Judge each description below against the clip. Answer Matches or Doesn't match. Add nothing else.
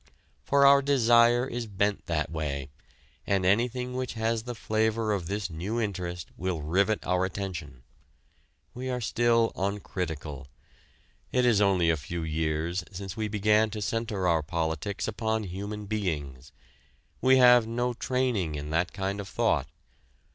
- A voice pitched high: Doesn't match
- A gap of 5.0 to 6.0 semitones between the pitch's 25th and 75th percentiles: Matches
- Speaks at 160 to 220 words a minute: Doesn't match